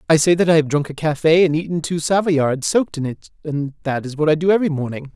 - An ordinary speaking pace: No, fast, 270 wpm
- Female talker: No, male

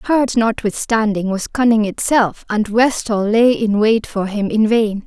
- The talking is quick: No, average, 165 wpm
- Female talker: Yes, female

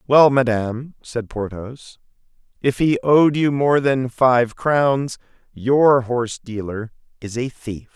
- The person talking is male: Yes, male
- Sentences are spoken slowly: Yes, slow, 130 wpm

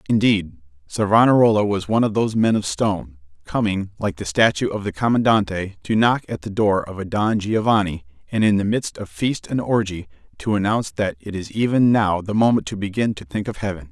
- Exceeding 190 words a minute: Yes, fast, 205 wpm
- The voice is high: No, low, 100 Hz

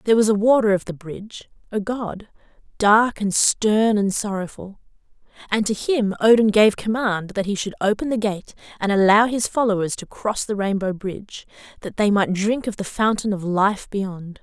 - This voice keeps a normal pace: Yes, average, 185 wpm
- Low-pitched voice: No, high, 205 Hz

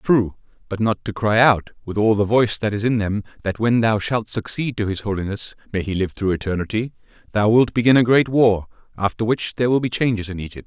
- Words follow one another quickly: Yes, fast, 220 wpm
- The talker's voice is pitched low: Yes, low, 110 Hz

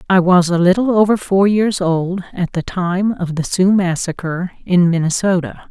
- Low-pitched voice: No, medium, 185 Hz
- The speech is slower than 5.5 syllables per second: Yes, 4.5 syllables/s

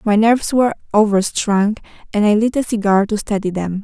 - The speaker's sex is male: No, female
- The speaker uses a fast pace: No, average, 190 wpm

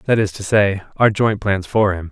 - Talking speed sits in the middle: No, fast, 255 wpm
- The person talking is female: No, male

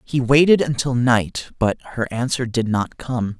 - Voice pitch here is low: Yes, low, 125 Hz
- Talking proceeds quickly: No, average, 175 wpm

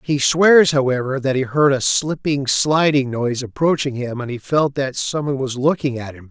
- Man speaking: Yes, male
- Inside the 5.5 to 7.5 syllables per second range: No, 5.0 syllables/s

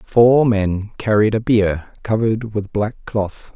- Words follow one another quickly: No, average, 150 wpm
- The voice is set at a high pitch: No, low, 105 Hz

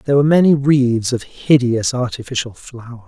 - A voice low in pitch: Yes, low, 125 Hz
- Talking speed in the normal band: Yes, average, 155 wpm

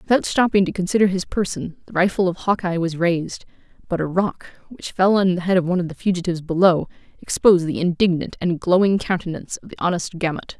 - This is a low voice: No, medium, 180 Hz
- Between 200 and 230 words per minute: Yes, fast, 205 wpm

